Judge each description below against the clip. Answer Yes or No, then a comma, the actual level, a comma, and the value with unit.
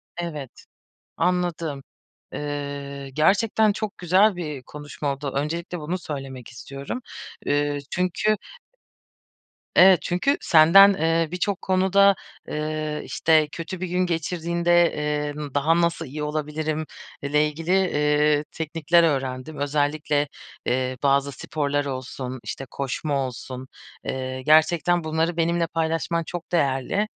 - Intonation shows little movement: No, average, 3.4 semitones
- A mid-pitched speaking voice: Yes, medium, 155 Hz